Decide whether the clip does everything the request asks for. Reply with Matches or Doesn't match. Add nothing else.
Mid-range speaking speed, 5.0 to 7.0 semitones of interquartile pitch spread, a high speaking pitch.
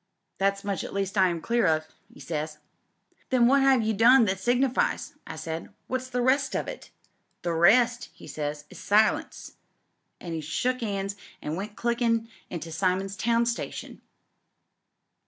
Matches